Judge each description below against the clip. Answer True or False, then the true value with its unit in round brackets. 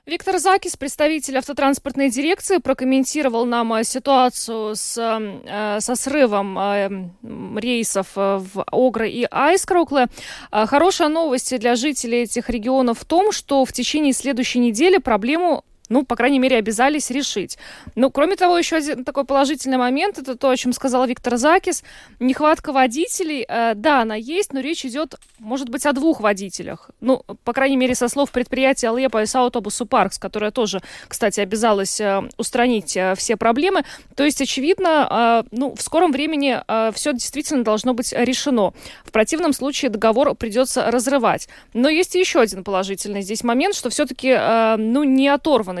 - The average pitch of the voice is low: False (255 Hz)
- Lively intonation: False (4.0 semitones)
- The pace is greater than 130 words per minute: True (155 wpm)